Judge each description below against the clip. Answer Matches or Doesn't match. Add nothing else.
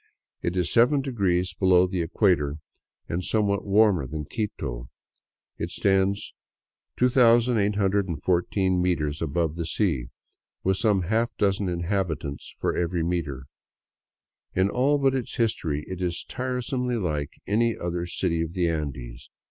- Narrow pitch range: Doesn't match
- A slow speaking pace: Matches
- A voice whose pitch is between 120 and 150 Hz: Doesn't match